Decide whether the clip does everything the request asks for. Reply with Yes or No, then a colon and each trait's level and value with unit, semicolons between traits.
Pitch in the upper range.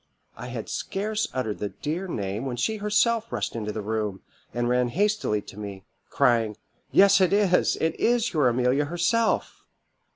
No: medium, 145 Hz